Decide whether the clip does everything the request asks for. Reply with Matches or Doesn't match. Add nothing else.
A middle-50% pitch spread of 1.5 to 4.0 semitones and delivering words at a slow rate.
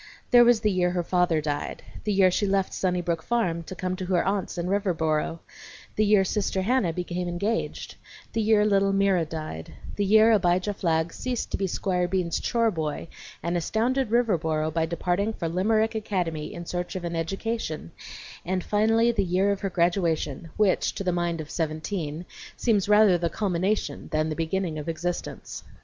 Doesn't match